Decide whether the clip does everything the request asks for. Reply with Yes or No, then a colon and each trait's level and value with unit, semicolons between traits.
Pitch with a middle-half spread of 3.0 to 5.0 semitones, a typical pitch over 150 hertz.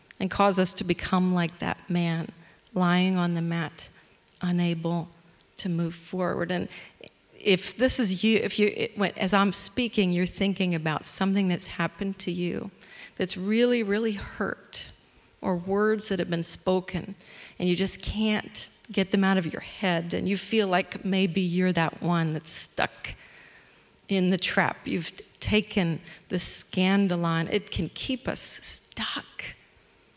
No: narrow, 2.5 semitones; medium, 185 Hz